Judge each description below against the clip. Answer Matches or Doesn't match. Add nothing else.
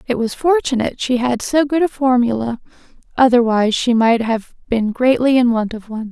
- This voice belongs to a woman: Matches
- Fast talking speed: Doesn't match